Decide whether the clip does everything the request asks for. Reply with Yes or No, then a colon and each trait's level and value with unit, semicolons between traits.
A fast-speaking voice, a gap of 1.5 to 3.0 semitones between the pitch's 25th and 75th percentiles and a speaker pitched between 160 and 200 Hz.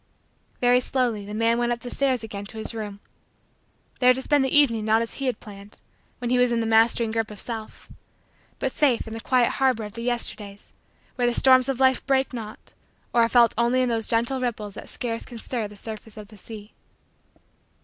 No: fast, 215 wpm; narrow, 2.4 semitones; high, 230 Hz